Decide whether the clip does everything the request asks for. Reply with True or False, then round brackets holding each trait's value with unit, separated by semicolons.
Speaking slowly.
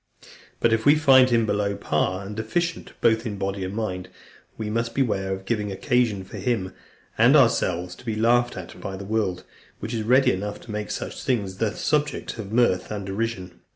False (195 wpm)